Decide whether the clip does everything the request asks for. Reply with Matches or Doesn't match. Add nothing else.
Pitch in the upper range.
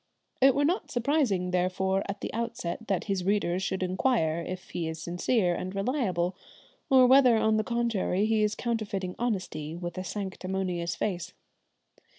Matches